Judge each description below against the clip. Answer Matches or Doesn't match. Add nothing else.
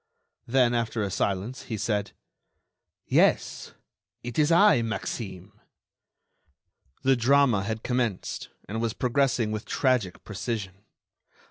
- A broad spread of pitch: Doesn't match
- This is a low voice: Matches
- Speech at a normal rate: Doesn't match